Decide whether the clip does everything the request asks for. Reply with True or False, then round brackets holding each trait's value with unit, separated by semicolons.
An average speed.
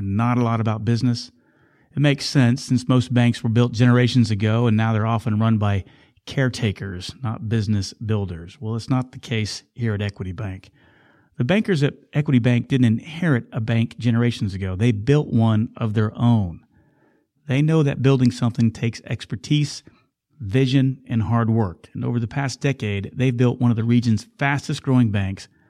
True (175 wpm)